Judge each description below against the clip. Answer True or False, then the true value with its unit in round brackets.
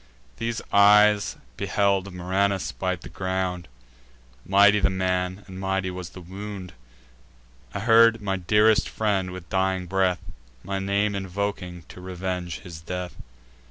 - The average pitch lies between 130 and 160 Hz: False (95 Hz)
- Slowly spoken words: True (130 wpm)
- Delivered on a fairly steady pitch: True (1.8 semitones)